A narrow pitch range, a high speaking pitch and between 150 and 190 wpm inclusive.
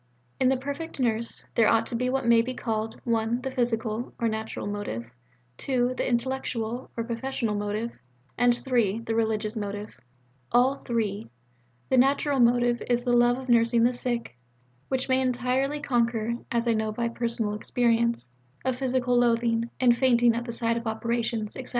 Yes: narrow, 1.8 semitones; high, 235 Hz; average, 170 wpm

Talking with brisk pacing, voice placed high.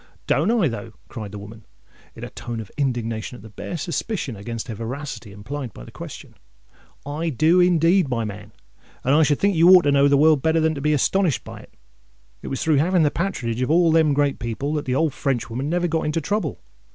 No: fast, 225 wpm; medium, 145 Hz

